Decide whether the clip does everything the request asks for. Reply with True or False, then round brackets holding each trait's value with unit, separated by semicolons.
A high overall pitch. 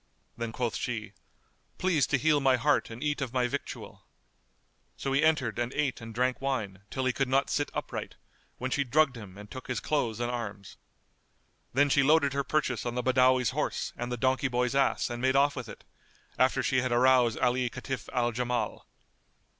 False (130 Hz)